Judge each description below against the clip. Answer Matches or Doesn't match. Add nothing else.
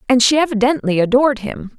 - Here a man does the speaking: Doesn't match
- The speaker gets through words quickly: Doesn't match